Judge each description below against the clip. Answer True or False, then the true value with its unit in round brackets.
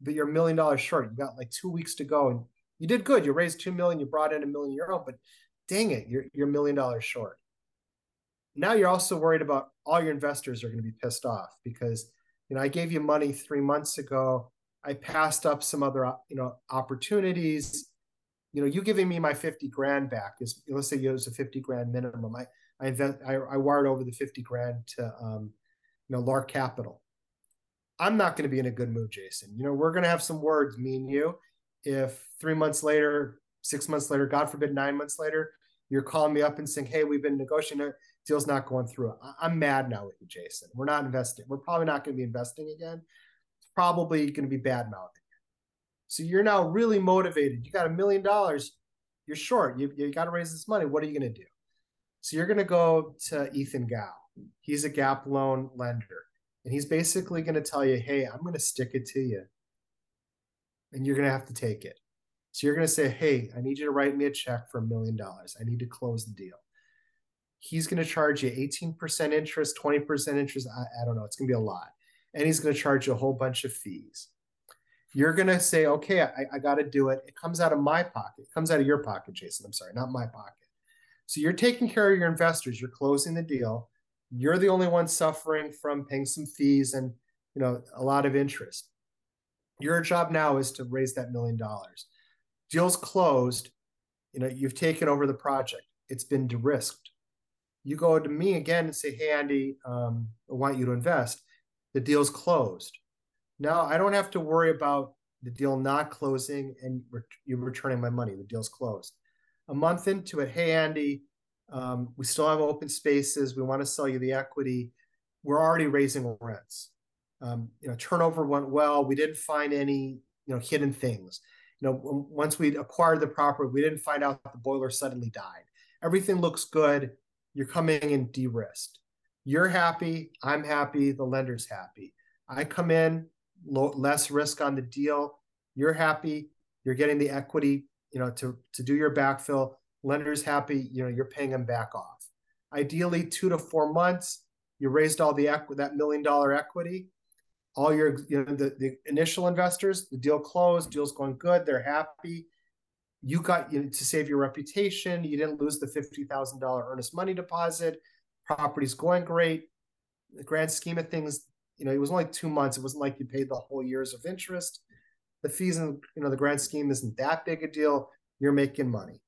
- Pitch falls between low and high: True (145 Hz)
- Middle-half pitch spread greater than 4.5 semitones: False (3.3 semitones)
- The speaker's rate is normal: False (210 wpm)